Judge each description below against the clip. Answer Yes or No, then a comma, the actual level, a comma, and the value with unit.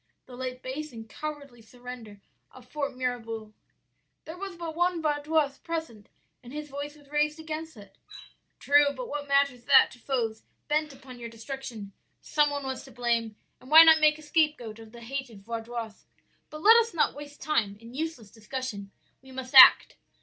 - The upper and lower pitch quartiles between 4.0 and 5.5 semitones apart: Yes, average, 4.5 semitones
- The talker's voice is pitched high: Yes, very high, 265 Hz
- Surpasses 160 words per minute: Yes, average, 180 wpm